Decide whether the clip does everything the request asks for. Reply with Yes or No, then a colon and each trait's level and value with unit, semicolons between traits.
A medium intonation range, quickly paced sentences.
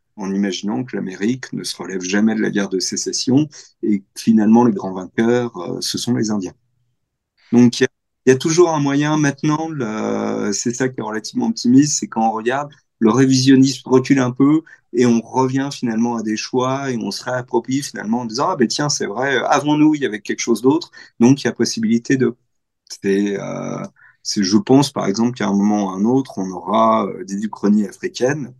No: average, 4.3 semitones; average, 210 wpm